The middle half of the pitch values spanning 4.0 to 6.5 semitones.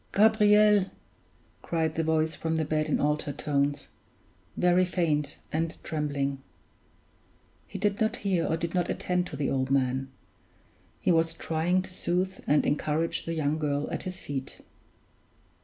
No: average, 3.5 semitones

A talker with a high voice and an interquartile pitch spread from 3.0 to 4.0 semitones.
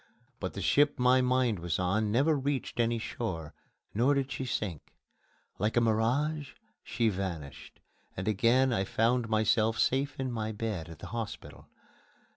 No: low, 115 Hz; average, 3.7 semitones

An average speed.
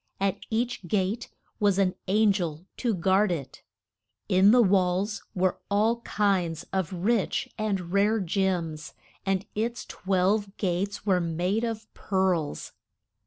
No: slow, 130 wpm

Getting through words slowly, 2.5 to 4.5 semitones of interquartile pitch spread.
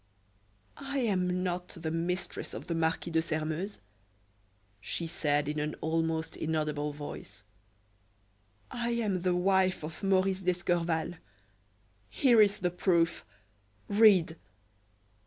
Yes: slow, 115 wpm; average, 2.9 semitones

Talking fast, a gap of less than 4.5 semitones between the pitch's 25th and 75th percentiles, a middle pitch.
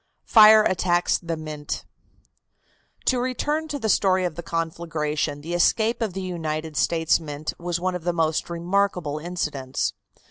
No: average, 150 wpm; average, 3.2 semitones; medium, 170 Hz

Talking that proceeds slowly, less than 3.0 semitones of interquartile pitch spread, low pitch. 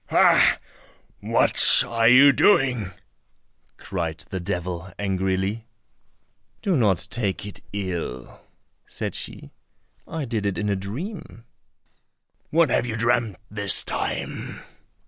No: slow, 110 wpm; average, 4.3 semitones; low, 105 Hz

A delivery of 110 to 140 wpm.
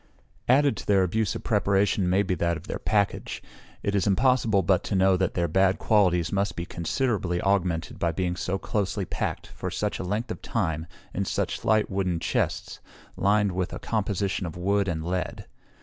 No: average, 190 wpm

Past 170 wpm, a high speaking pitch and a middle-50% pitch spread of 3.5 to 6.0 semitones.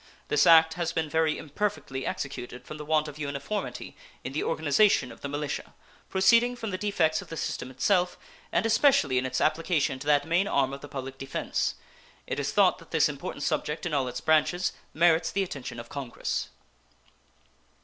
No: average, 185 wpm; medium, 155 Hz; average, 4.2 semitones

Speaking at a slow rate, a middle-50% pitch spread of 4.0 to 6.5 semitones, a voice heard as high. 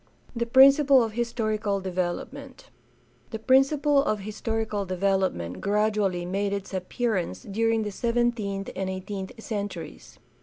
No: slow, 120 wpm; average, 3.4 semitones; high, 210 Hz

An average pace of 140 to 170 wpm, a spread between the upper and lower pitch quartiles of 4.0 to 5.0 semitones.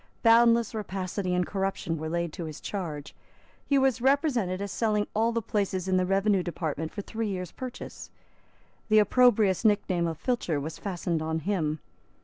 Yes: average, 165 wpm; average, 4.6 semitones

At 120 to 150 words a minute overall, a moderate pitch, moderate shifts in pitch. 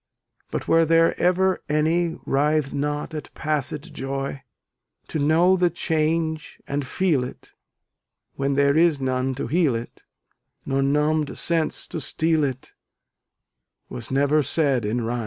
Yes: average, 140 wpm; medium, 150 Hz; average, 3.0 semitones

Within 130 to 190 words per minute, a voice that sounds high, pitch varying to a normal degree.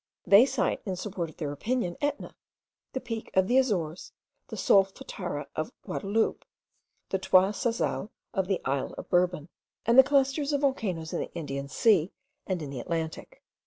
No: average, 165 wpm; high, 195 Hz; wide, 6.4 semitones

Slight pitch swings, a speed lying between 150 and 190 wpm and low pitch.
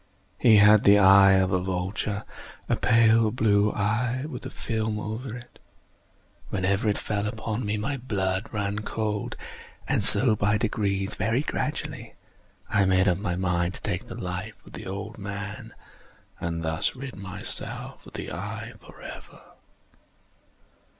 No: narrow, 2.2 semitones; average, 140 wpm; low, 105 Hz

